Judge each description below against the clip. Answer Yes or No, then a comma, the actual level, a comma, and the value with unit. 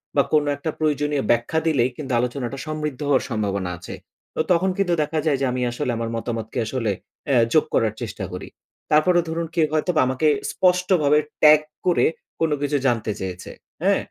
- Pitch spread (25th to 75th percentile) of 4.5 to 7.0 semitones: Yes, average, 4.8 semitones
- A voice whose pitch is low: No, medium, 145 Hz